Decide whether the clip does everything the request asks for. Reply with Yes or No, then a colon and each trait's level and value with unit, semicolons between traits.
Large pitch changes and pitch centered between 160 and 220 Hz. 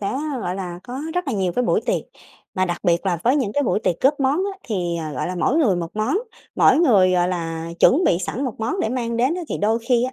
Yes: wide, 6.5 semitones; high, 215 Hz